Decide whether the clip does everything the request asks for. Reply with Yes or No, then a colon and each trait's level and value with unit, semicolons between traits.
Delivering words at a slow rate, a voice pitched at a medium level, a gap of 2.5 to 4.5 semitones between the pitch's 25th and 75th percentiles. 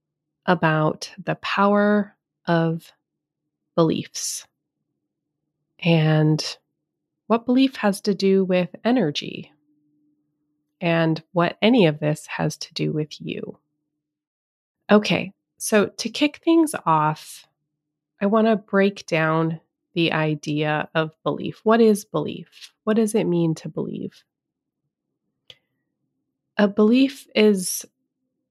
No: slow, 105 wpm; medium, 170 Hz; average, 5.3 semitones